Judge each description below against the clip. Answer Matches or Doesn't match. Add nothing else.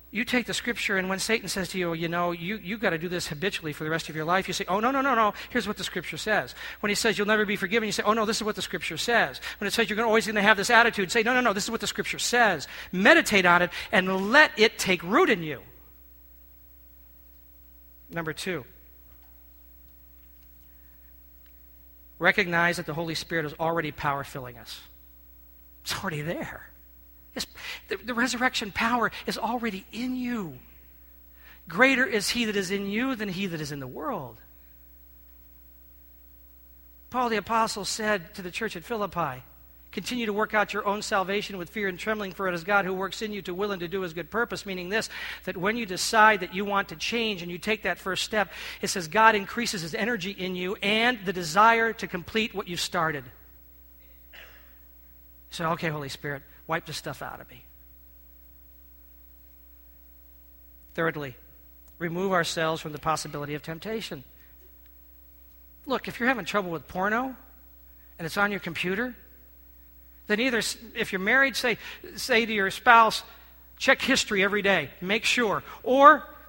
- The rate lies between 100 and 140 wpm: Doesn't match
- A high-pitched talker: Doesn't match